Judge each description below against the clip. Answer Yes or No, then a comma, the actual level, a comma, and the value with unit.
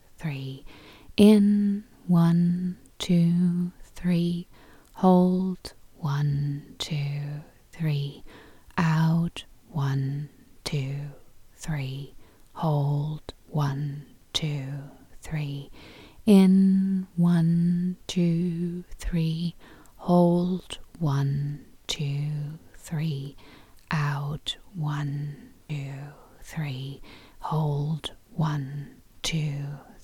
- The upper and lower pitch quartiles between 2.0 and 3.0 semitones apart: No, average, 3.5 semitones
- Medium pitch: Yes, medium, 155 Hz